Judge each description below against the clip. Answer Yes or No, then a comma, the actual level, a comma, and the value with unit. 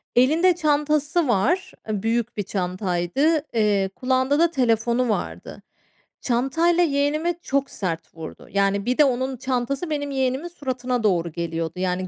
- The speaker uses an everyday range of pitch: No, wide, 6.5 semitones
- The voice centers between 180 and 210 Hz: No, very high, 255 Hz